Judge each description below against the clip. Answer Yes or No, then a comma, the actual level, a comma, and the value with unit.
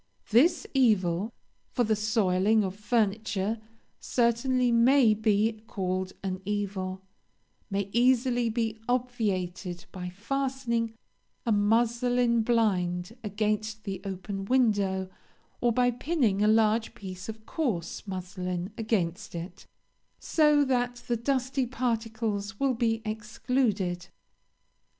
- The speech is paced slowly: Yes, slow, 110 wpm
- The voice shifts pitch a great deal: No, average, 3.7 semitones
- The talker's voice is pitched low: No, high, 220 Hz